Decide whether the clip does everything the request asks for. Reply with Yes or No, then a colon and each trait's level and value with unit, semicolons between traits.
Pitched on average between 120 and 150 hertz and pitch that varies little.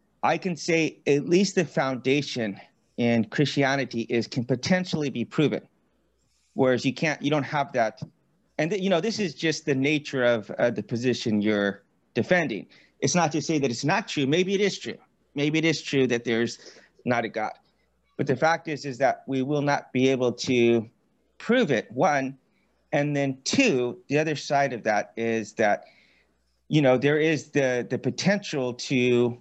No: medium, 140 Hz; average, 4.2 semitones